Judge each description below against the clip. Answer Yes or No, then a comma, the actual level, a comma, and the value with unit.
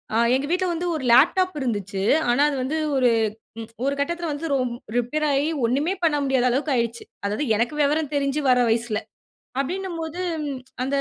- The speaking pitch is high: Yes, very high, 280 Hz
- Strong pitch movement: No, average, 4.4 semitones